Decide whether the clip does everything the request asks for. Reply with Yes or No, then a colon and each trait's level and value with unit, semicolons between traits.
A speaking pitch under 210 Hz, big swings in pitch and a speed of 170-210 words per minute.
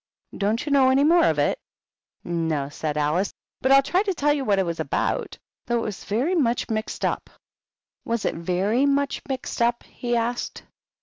No: high, 235 Hz; wide, 6.3 semitones; average, 200 wpm